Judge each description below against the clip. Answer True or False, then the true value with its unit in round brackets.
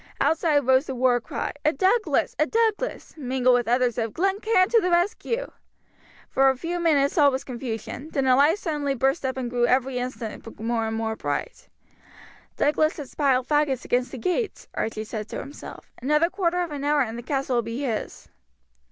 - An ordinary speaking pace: True (195 wpm)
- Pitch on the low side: False (270 Hz)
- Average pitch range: True (4.7 semitones)